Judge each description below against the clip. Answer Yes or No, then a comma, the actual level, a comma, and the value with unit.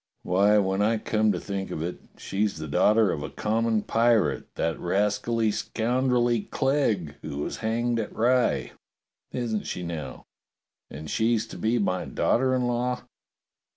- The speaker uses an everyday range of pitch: Yes, average, 3.8 semitones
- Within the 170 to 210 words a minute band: No, average, 155 wpm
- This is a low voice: Yes, low, 110 Hz